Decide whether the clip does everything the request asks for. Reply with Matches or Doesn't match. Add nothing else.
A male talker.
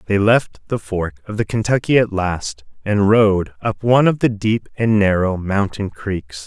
Matches